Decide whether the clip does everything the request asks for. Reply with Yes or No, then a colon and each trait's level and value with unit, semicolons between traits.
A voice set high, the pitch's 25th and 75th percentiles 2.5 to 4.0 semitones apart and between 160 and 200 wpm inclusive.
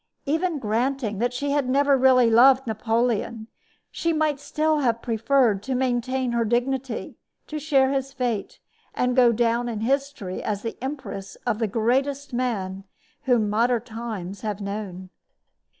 No: high, 245 Hz; average, 3.5 semitones; average, 150 wpm